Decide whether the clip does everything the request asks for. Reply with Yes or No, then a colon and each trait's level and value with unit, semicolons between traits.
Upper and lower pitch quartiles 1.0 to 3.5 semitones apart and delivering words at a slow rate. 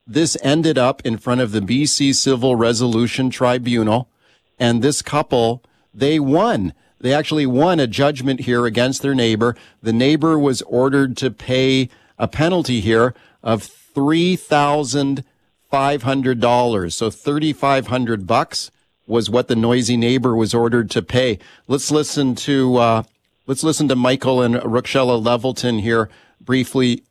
No: average, 2.8 semitones; average, 150 wpm